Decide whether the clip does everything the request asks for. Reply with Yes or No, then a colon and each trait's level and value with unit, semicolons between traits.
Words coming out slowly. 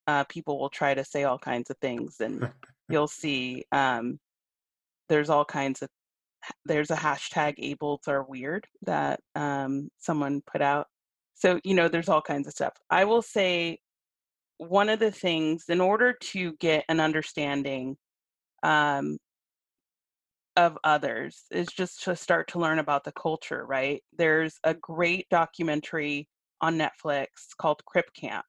No: average, 150 wpm